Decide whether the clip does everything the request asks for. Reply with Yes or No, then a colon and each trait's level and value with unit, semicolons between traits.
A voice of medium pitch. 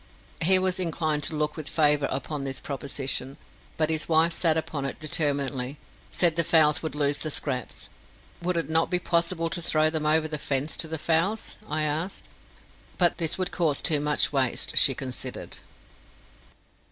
Yes: medium, 155 Hz